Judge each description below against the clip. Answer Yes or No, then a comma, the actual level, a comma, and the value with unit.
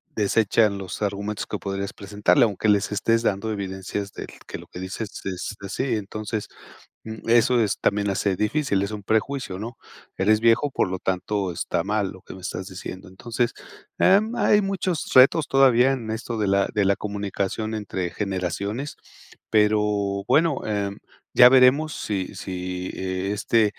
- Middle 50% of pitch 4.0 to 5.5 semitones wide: No, average, 2.8 semitones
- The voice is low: Yes, low, 105 Hz